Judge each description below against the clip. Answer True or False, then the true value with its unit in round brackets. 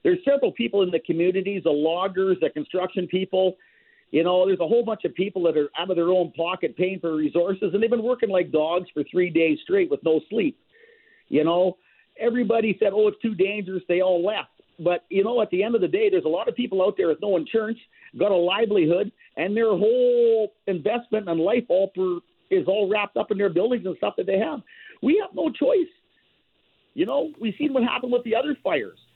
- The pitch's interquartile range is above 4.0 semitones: True (5.6 semitones)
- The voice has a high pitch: True (200 Hz)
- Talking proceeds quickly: True (225 wpm)